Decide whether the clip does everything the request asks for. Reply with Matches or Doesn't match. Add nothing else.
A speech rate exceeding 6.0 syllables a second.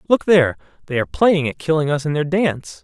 Matches